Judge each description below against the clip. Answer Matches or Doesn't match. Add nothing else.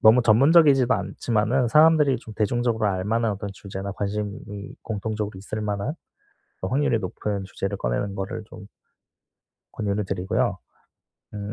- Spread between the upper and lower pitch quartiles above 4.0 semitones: Doesn't match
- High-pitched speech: Doesn't match